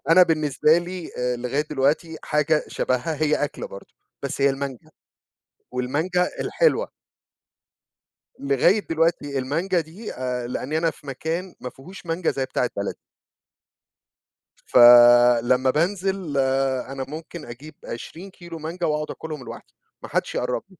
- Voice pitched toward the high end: No, medium, 150 Hz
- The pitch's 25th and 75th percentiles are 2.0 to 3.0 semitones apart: No, average, 4.6 semitones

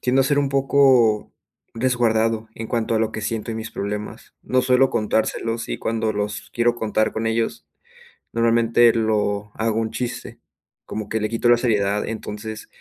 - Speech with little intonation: Yes, narrow, 1.6 semitones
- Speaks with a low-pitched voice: Yes, low, 115 Hz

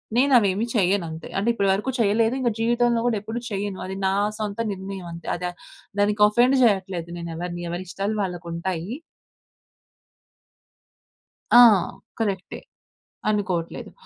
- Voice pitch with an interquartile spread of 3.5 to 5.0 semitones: Yes, average, 3.8 semitones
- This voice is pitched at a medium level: No, high, 195 Hz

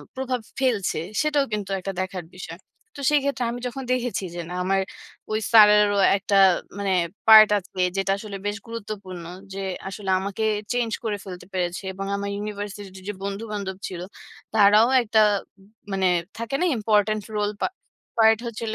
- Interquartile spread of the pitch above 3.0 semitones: No, narrow, 2.5 semitones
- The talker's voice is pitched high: Yes, high, 210 Hz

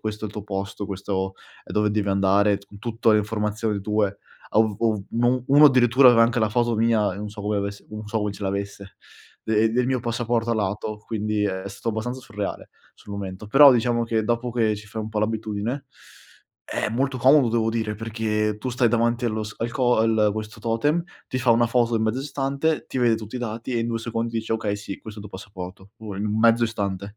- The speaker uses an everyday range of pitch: No, narrow, 2.2 semitones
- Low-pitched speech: Yes, low, 110 Hz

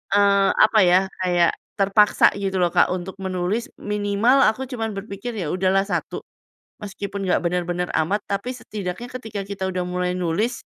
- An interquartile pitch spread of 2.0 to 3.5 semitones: Yes, narrow, 2.6 semitones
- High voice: Yes, high, 195 Hz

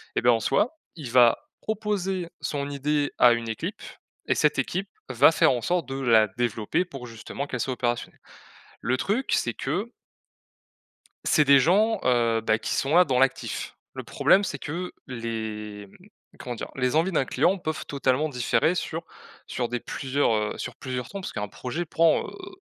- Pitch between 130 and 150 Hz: Yes, low, 135 Hz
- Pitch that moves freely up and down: Yes, wide, 6.3 semitones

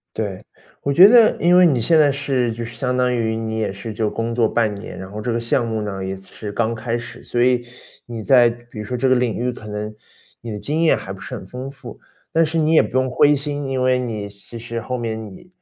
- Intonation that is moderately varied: Yes, average, 3.3 semitones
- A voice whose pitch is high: No, low, 120 Hz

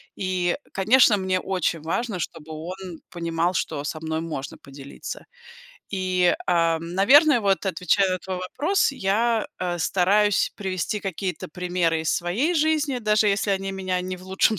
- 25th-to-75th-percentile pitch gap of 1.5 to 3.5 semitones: Yes, average, 3.2 semitones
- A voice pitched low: No, medium, 185 Hz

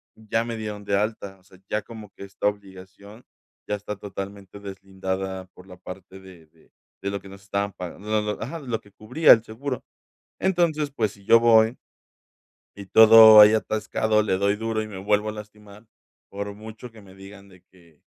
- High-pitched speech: No, low, 105 Hz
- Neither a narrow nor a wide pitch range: No, narrow, 2.1 semitones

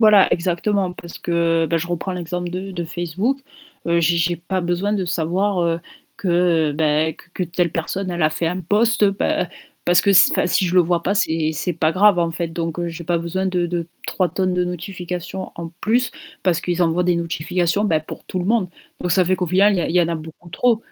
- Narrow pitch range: Yes, narrow, 1.9 semitones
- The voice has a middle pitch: Yes, medium, 175 Hz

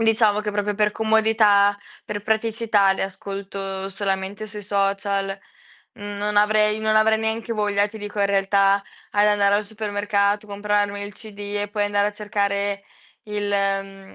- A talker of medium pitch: No, high, 205 Hz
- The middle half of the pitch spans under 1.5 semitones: Yes, narrow, 1.0 semitones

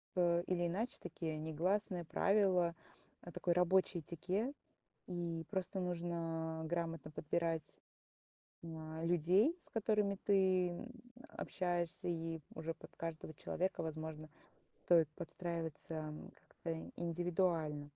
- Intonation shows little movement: Yes, narrow, 2.1 semitones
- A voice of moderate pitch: Yes, medium, 170 Hz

